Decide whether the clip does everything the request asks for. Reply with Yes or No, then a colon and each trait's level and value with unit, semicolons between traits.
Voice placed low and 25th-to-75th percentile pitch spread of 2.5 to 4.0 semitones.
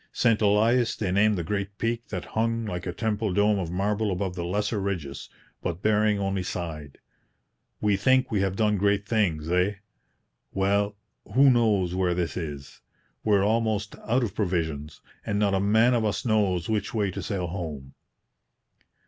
Yes: low, 100 Hz; average, 3.2 semitones